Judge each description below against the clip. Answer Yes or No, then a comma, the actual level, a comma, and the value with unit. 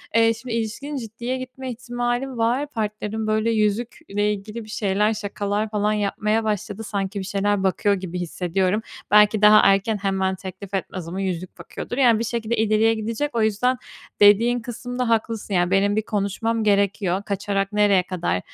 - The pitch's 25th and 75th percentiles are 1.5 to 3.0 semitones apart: Yes, narrow, 2.4 semitones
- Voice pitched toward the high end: Yes, high, 210 Hz